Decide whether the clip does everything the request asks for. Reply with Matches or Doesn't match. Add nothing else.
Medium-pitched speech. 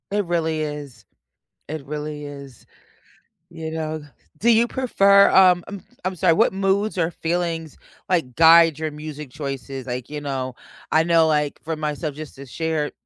Matches